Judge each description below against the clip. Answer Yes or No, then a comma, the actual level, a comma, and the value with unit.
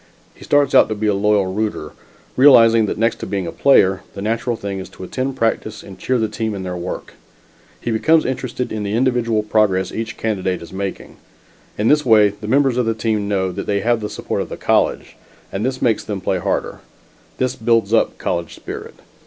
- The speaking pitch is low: Yes, low, 110 Hz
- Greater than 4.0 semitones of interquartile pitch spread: No, average, 3.1 semitones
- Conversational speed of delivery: No, fast, 210 wpm